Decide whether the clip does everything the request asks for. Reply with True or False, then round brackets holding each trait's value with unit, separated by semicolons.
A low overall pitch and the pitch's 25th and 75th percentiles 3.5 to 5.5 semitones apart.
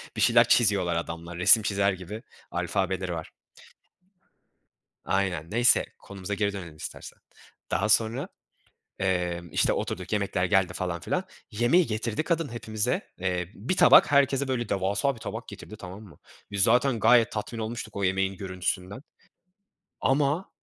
True (100 Hz; 4.2 semitones)